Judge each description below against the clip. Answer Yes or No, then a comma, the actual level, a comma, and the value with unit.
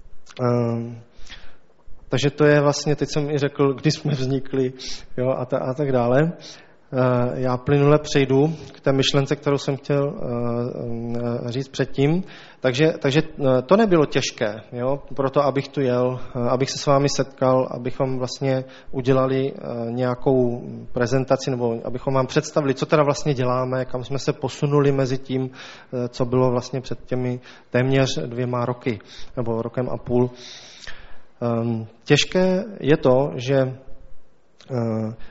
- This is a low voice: Yes, low, 130 Hz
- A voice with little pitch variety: Yes, narrow, 2.3 semitones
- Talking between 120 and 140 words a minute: Yes, average, 135 wpm